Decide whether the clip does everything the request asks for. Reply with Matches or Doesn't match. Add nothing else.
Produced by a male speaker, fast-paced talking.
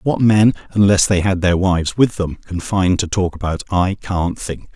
Matches